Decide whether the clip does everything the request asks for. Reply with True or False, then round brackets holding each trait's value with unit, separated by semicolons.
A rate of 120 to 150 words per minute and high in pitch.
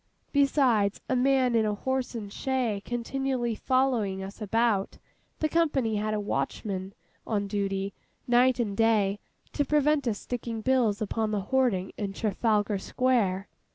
True (145 wpm; 225 Hz)